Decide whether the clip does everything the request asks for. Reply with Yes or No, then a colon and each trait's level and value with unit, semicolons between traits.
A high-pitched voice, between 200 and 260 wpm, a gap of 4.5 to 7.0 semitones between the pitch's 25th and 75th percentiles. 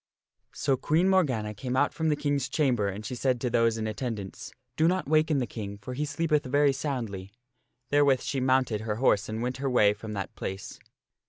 No: low, 130 Hz; fast, 205 wpm; average, 4.8 semitones